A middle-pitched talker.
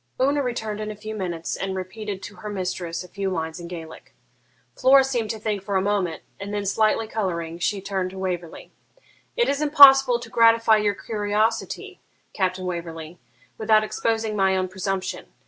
No: high, 205 Hz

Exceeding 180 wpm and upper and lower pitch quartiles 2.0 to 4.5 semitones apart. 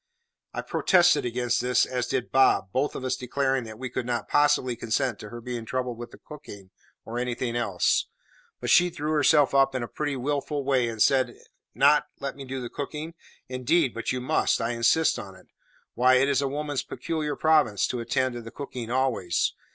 Yes: average, 200 wpm; average, 2.9 semitones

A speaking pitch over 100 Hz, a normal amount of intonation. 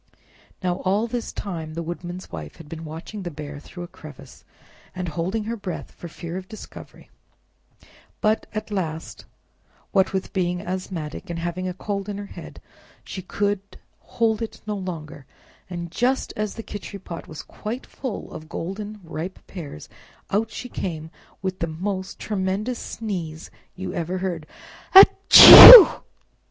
Yes: medium, 185 Hz; average, 3.8 semitones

